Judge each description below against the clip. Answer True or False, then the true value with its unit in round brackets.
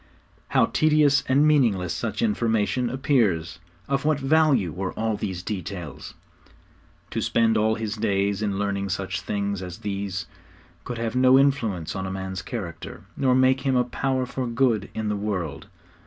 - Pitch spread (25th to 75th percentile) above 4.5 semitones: True (5.1 semitones)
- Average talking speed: True (160 wpm)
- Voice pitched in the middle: False (110 Hz)